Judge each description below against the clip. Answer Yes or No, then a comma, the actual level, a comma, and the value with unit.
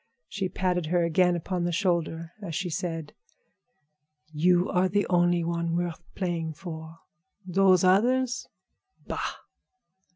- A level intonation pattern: Yes, narrow, 1.8 semitones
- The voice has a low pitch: No, medium, 175 Hz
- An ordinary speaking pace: No, slow, 125 wpm